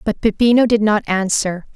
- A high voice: Yes, high, 210 Hz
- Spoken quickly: No, average, 170 wpm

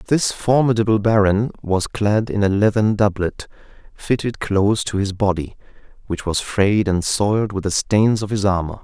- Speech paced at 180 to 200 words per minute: No, average, 170 wpm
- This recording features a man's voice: Yes, male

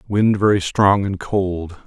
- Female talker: No, male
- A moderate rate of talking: Yes, average, 160 wpm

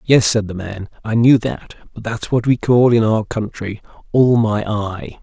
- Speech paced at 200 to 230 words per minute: Yes, fast, 205 wpm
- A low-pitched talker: Yes, low, 110 Hz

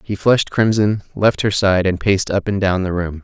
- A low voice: Yes, very low, 95 Hz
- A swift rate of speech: Yes, fast, 240 wpm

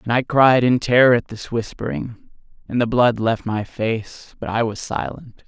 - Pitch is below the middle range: Yes, low, 115 Hz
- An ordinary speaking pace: Yes, average, 195 wpm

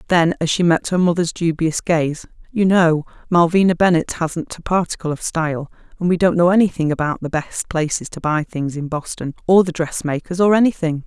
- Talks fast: No, average, 195 wpm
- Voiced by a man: No, female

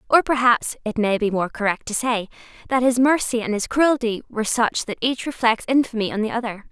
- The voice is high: Yes, high, 235 Hz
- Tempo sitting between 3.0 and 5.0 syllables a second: No, 5.6 syllables/s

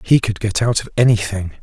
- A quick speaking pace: Yes, fast, 220 wpm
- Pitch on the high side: No, low, 105 Hz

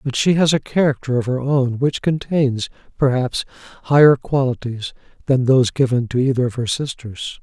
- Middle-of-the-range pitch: No, low, 130 Hz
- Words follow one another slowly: No, average, 170 wpm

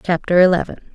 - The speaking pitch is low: No, medium, 175 Hz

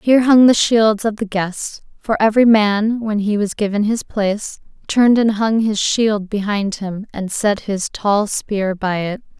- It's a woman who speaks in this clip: Yes, female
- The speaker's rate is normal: Yes, average, 190 wpm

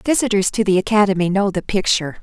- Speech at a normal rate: Yes, average, 190 wpm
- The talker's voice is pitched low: No, high, 195 Hz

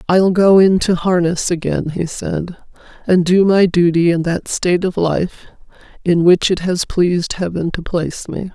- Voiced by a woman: Yes, female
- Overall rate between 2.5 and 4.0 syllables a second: No, 4.5 syllables/s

